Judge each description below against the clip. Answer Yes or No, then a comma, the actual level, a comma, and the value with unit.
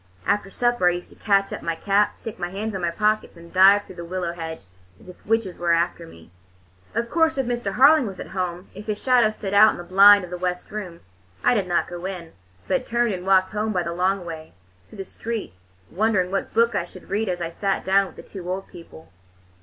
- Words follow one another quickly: Yes, fast, 240 wpm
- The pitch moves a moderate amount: Yes, average, 3.3 semitones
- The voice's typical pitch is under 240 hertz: Yes, high, 190 Hz